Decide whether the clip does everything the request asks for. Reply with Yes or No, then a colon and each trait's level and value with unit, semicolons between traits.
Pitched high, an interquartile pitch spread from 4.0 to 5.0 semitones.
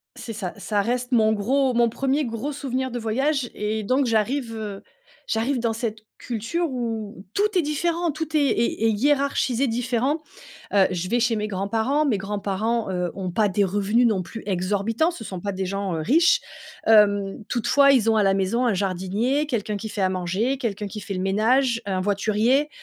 Yes: high, 225 Hz; average, 4.5 semitones